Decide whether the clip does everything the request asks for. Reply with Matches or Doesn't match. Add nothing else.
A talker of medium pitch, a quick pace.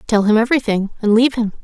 Doesn't match